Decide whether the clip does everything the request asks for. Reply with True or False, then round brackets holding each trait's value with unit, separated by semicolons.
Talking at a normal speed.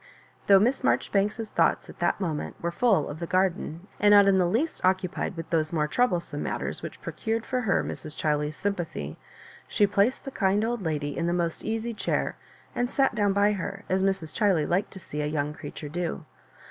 False (210 wpm)